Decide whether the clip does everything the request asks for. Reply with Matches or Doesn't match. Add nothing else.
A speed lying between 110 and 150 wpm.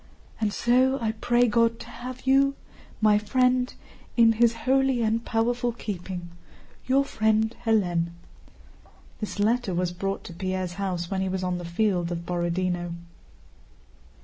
Matches